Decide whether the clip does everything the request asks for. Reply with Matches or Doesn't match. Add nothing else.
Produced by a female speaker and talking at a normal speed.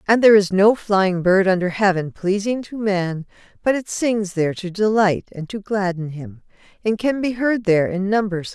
Doesn't match